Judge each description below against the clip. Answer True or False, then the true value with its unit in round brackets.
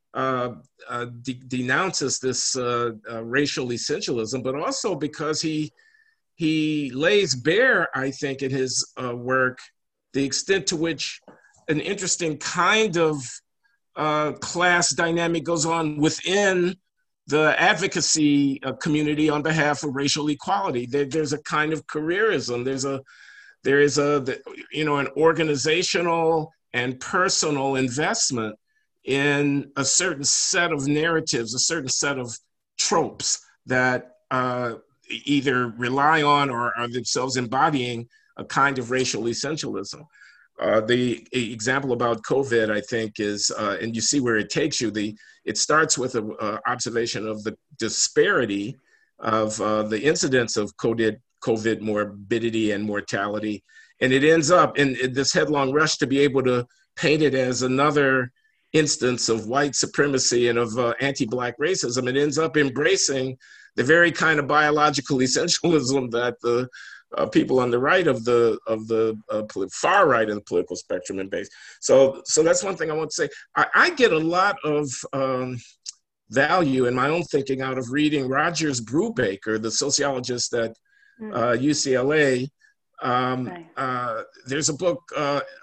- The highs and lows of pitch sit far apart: False (4.0 semitones)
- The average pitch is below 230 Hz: True (140 Hz)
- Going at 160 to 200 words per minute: False (150 wpm)